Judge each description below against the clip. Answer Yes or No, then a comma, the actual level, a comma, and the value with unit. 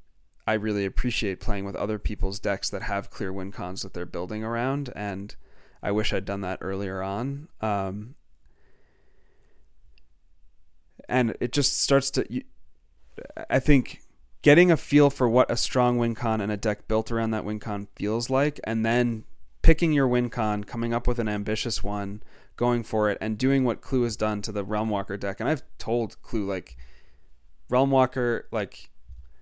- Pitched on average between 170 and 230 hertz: No, low, 105 Hz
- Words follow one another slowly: No, average, 170 wpm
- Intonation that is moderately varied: Yes, average, 4.0 semitones